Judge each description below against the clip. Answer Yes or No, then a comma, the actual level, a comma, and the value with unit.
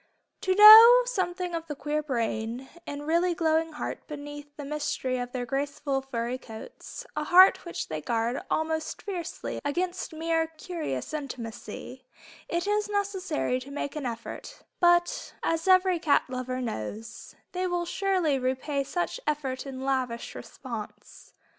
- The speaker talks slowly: No, average, 145 wpm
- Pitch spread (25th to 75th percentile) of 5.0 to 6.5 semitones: Yes, average, 5.3 semitones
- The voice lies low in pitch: No, very high, 300 Hz